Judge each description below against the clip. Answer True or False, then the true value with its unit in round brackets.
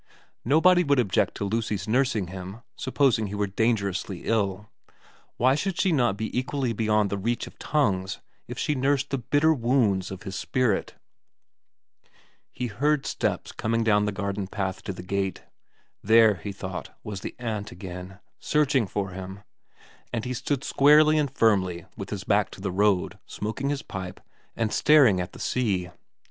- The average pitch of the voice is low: True (110 Hz)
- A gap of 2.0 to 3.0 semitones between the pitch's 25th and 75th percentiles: False (5.0 semitones)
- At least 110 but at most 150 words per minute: False (165 wpm)